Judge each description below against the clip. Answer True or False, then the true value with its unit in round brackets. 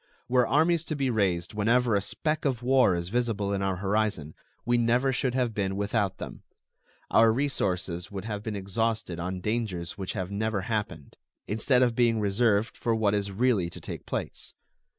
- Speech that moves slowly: False (180 wpm)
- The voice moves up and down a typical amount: True (3.7 semitones)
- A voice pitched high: False (110 Hz)